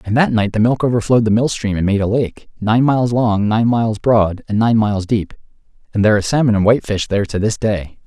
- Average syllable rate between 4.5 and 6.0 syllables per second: No, 6.2 syllables/s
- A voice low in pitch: Yes, low, 110 Hz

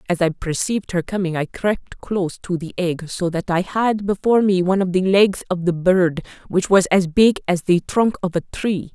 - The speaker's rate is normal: No, fast, 230 wpm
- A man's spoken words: No, female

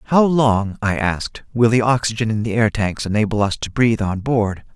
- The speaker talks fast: Yes, fast, 215 wpm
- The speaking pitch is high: No, low, 110 Hz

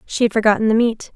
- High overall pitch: Yes, high, 220 Hz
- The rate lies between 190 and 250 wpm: No, fast, 260 wpm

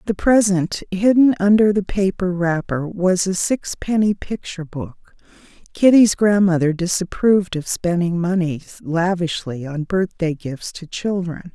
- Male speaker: No, female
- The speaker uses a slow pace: Yes, slow, 125 wpm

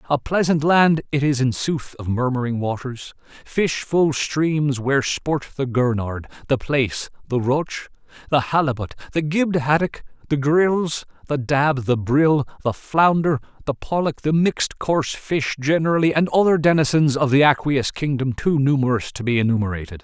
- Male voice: Yes, male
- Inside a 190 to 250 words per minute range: No, average, 155 wpm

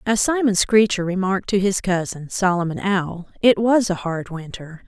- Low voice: No, high, 190 Hz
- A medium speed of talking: Yes, average, 170 wpm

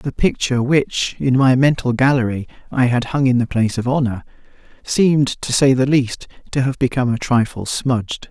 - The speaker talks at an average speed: Yes, average, 190 wpm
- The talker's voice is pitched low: Yes, low, 130 Hz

